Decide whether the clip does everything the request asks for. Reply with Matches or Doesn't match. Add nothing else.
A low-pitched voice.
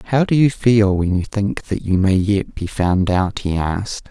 Matches